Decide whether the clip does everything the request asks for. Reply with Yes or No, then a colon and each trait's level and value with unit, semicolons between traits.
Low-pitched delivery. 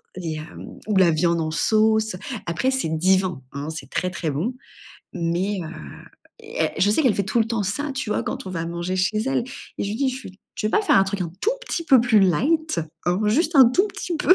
No: high, 200 Hz